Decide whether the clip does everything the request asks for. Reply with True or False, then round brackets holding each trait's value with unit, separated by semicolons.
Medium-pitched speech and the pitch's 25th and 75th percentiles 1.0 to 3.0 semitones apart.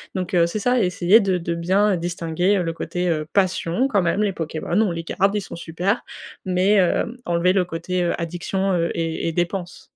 True (180 Hz; 2.5 semitones)